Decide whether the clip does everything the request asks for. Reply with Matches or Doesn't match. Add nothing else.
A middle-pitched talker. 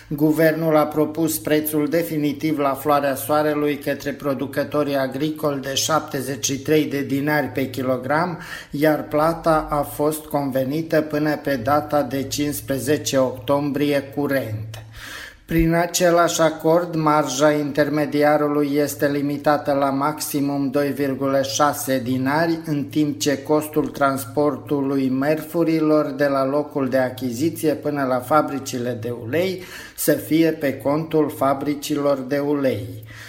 Matches